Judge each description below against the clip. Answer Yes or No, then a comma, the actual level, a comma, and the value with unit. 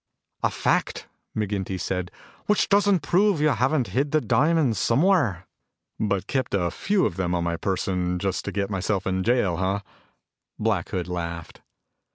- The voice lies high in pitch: No, low, 100 Hz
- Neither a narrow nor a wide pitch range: No, wide, 7.4 semitones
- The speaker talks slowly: No, average, 160 wpm